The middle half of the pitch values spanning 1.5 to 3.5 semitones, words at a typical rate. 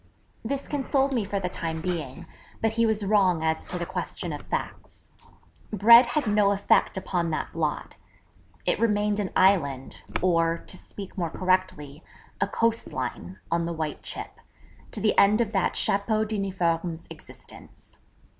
No: average, 4.2 semitones; average, 155 wpm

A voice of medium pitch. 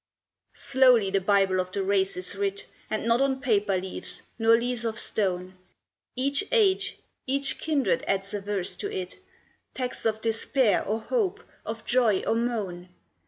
No: high, 225 Hz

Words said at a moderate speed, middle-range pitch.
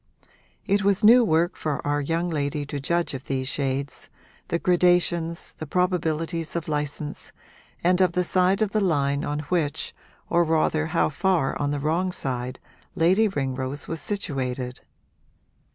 Yes: average, 150 wpm; medium, 160 Hz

